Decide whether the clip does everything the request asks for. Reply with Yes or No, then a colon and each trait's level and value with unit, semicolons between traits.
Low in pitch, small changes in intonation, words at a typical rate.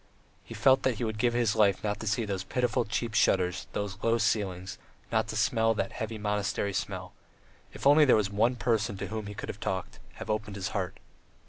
No: low, 105 Hz; narrow, 2.3 semitones; fast, 215 wpm